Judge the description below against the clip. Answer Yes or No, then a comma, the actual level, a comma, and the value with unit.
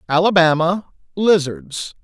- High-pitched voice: No, medium, 175 Hz